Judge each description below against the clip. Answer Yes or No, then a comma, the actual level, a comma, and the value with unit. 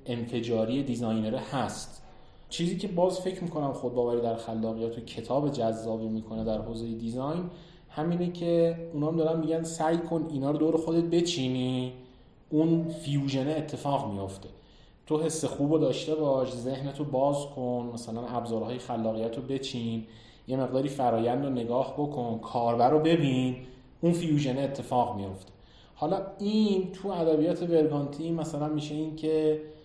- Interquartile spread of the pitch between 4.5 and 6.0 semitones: Yes, average, 4.9 semitones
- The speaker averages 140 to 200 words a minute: Yes, average, 145 wpm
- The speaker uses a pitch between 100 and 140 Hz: Yes, low, 135 Hz